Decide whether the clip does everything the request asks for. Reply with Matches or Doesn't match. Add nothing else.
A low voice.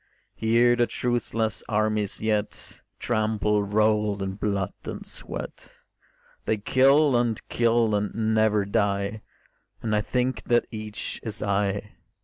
Matches